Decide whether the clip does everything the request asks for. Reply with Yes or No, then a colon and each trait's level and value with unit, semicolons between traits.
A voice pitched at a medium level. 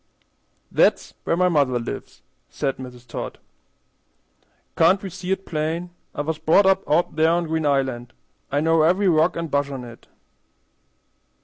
Yes: medium, 160 Hz